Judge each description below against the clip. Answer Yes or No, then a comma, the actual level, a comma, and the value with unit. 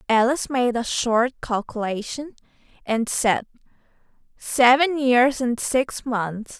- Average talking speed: No, slow, 110 wpm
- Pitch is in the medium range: No, high, 245 Hz